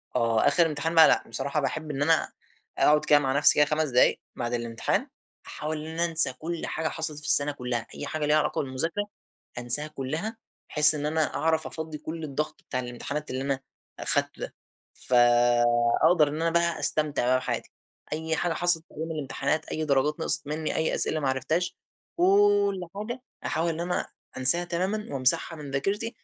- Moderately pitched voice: Yes, medium, 155 Hz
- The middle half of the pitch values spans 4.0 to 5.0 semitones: No, average, 3.3 semitones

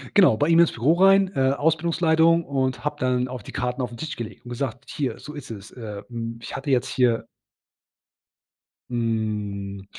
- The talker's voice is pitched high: No, low, 125 Hz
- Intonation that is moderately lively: Yes, average, 4.7 semitones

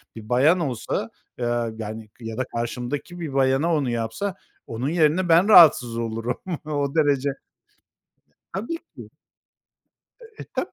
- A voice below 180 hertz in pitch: Yes, low, 135 Hz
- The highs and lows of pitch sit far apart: Yes, wide, 5.8 semitones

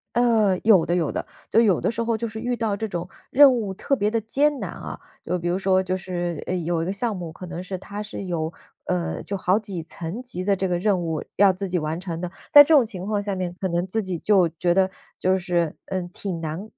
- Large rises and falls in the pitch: No, average, 3.5 semitones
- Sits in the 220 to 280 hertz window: No, high, 190 Hz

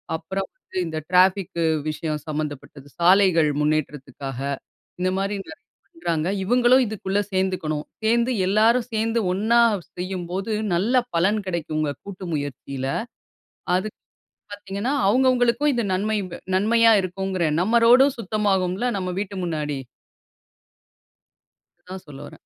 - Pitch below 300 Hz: Yes, high, 190 Hz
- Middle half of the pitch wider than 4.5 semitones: Yes, average, 5.1 semitones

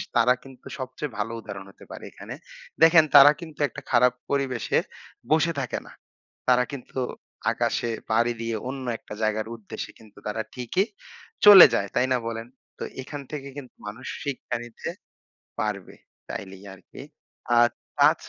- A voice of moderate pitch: No, low, 125 Hz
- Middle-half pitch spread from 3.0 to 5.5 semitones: Yes, average, 3.7 semitones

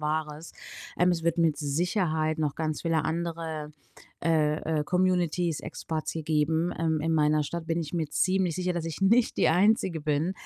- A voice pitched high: No, medium, 160 Hz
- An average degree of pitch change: No, narrow, 2.0 semitones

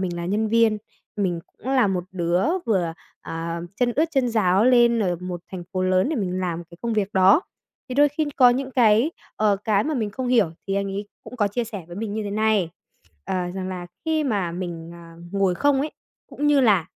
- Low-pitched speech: No, high, 205 Hz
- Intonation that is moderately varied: Yes, average, 4.9 semitones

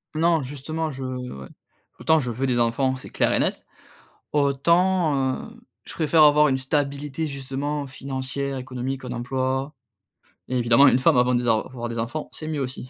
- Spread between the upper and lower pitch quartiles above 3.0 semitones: No, average, 2.7 semitones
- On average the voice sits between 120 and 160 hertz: Yes, low, 135 Hz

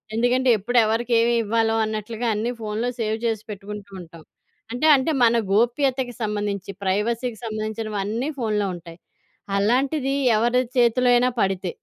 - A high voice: Yes, high, 225 Hz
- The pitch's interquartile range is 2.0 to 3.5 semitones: Yes, average, 2.7 semitones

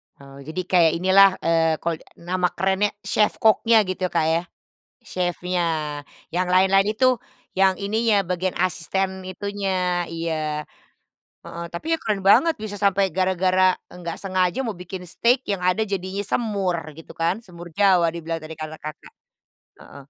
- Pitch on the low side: No, medium, 185 Hz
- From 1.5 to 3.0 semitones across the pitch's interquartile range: Yes, average, 2.7 semitones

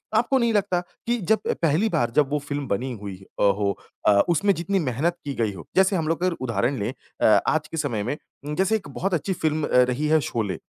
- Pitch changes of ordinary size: No, wide, 7.4 semitones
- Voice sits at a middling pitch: Yes, medium, 150 Hz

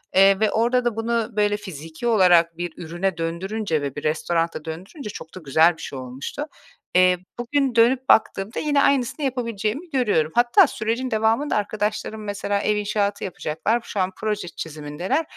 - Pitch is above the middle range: Yes, high, 205 Hz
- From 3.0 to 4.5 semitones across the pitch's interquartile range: No, wide, 5.5 semitones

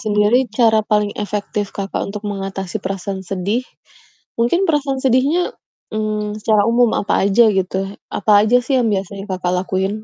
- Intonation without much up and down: No, average, 3.3 semitones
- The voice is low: No, high, 210 Hz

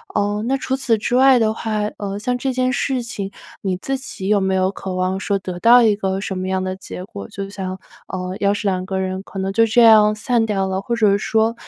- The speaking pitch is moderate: No, high, 205 Hz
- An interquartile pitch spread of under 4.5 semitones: Yes, average, 3.2 semitones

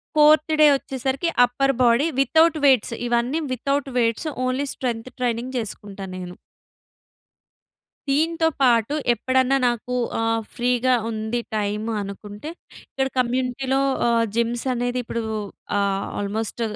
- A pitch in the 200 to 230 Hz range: No, high, 245 Hz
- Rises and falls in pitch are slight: No, average, 3.1 semitones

